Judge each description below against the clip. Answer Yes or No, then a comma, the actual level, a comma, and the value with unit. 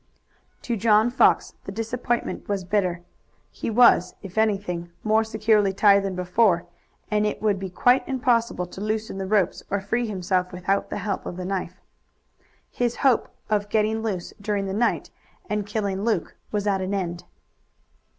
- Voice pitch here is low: No, high, 205 Hz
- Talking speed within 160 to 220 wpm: Yes, average, 165 wpm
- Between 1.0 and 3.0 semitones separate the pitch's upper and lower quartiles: Yes, average, 2.7 semitones